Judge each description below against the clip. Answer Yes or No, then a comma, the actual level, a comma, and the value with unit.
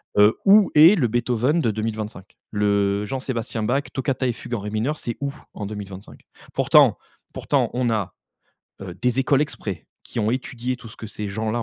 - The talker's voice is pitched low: Yes, low, 115 Hz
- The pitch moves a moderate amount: Yes, average, 3.7 semitones